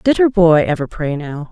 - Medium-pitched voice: Yes, medium, 170 Hz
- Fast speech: Yes, fast, 240 wpm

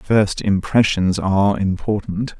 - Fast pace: No, slow, 100 wpm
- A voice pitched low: Yes, low, 100 Hz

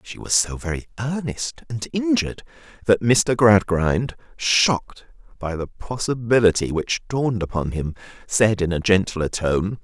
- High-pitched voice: No, low, 105 Hz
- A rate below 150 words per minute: Yes, average, 140 wpm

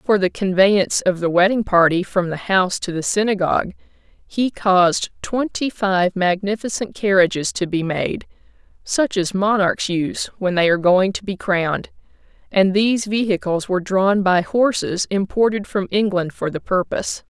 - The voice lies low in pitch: No, high, 190 Hz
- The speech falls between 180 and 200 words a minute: No, average, 160 wpm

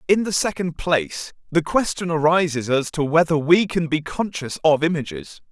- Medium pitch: Yes, medium, 160 Hz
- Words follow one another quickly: No, average, 175 wpm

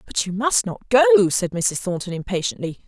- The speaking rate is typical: Yes, average, 190 wpm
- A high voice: Yes, high, 205 Hz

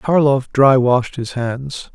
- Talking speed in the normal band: Yes, average, 155 wpm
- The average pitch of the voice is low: Yes, low, 130 Hz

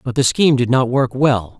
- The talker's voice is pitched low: Yes, low, 125 Hz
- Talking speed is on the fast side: Yes, fast, 265 wpm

